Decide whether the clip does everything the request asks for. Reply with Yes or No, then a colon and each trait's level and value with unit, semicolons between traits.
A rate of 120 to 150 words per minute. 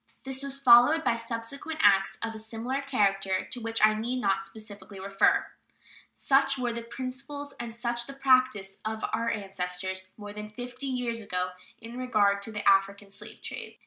No: average, 175 wpm